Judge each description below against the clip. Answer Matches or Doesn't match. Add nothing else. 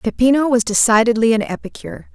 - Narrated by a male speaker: Doesn't match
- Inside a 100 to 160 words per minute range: Matches